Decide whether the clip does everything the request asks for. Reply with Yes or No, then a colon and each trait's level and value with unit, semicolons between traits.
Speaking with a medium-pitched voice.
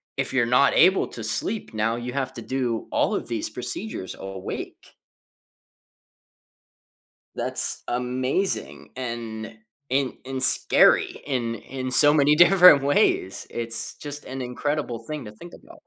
No: low, 130 Hz